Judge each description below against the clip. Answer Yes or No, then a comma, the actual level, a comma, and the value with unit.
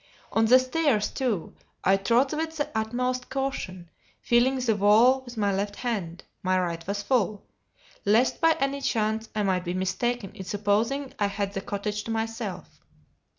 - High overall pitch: Yes, high, 220 Hz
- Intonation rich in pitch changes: No, average, 4.1 semitones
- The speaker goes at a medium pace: Yes, average, 165 wpm